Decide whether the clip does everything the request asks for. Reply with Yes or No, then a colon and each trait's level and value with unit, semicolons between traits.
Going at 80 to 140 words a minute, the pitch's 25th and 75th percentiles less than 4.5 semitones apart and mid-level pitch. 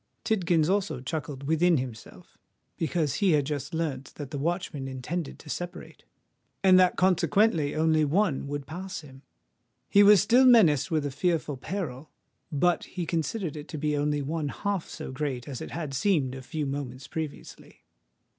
No: average, 165 wpm; average, 4.1 semitones; medium, 155 Hz